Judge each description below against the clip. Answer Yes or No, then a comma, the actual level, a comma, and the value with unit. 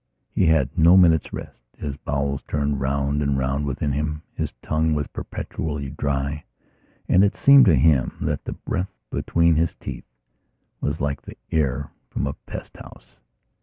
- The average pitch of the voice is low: Yes, very low, 75 Hz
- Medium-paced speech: Yes, average, 160 wpm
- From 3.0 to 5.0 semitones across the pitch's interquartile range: No, narrow, 2.5 semitones